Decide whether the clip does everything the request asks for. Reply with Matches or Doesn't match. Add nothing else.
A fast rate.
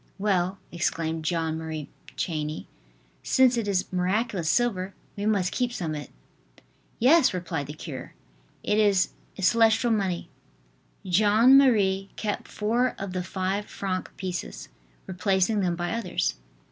Doesn't match